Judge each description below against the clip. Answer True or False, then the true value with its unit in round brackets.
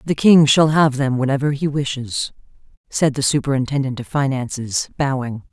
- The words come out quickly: False (150 wpm)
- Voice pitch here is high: False (135 Hz)